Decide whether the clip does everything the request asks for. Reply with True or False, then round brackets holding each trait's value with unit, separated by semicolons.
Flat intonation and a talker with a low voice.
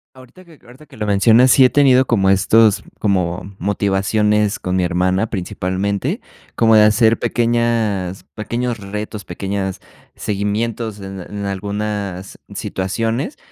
False (3.1 semitones; 105 Hz)